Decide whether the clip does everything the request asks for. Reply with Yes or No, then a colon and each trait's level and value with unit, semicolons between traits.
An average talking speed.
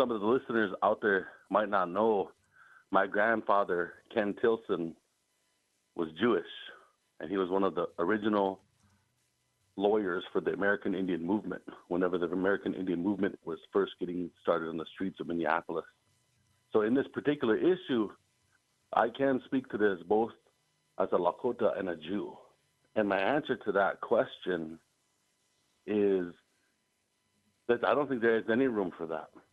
Yes: average, 155 wpm